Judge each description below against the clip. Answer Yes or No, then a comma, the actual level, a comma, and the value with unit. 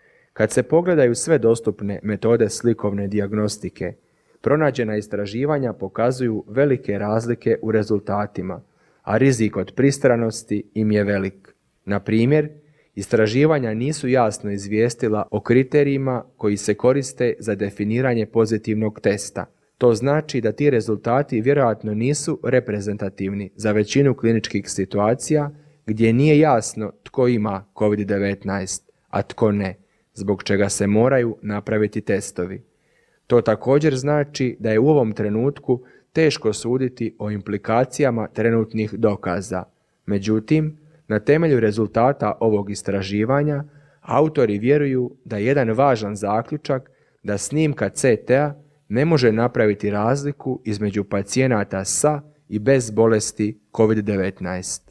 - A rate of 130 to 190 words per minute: No, average, 115 wpm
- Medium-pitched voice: No, low, 110 Hz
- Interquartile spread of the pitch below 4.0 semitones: No, average, 4.4 semitones